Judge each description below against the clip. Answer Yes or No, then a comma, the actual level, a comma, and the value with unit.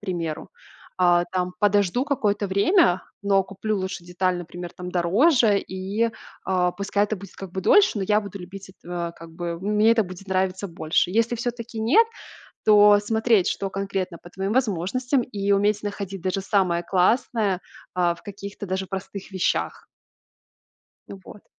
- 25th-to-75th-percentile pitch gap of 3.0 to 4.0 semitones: No, narrow, 2.6 semitones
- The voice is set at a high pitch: Yes, high, 195 Hz